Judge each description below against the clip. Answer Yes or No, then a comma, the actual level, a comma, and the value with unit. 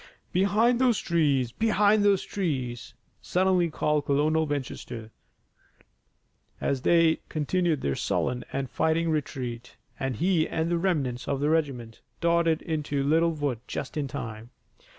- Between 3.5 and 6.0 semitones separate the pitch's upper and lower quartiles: Yes, average, 4.3 semitones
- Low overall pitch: No, medium, 155 Hz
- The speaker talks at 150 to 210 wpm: No, slow, 135 wpm